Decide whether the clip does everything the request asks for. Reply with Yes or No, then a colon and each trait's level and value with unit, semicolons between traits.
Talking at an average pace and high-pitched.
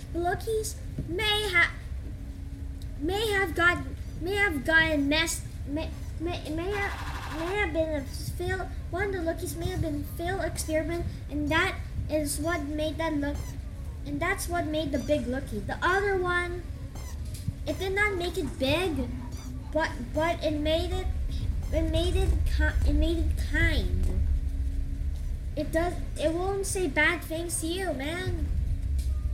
Yes: average, 155 wpm; very high, 315 Hz